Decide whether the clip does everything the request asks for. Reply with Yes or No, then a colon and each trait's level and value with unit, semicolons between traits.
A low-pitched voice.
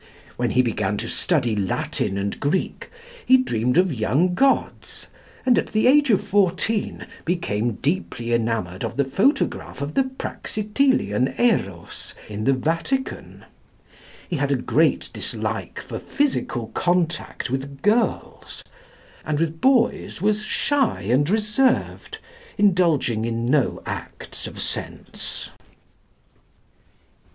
No: medium, 160 Hz